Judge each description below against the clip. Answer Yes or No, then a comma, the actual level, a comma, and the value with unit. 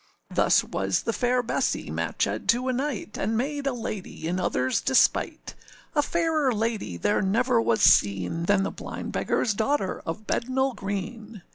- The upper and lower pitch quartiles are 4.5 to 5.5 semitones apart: Yes, average, 5.1 semitones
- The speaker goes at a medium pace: Yes, average, 160 wpm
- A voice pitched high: Yes, high, 225 Hz